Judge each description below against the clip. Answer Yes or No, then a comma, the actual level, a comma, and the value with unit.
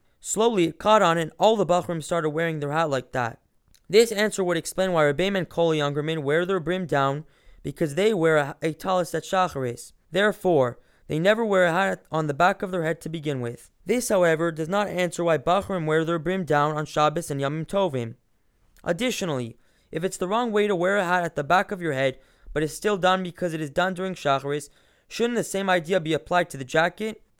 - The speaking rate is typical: No, fast, 220 wpm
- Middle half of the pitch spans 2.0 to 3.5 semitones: No, average, 4.1 semitones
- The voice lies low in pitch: No, medium, 170 Hz